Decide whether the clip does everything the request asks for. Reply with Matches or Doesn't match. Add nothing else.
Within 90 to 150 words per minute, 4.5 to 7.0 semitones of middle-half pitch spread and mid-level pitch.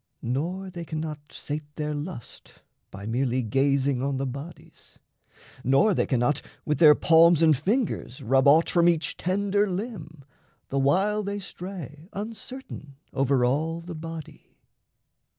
Matches